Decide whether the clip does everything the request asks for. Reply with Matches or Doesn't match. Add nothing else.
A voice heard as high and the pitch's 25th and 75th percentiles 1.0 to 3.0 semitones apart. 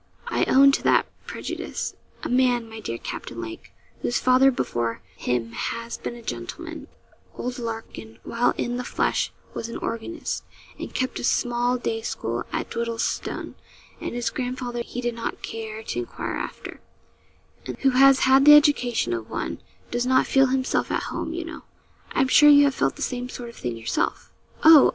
Matches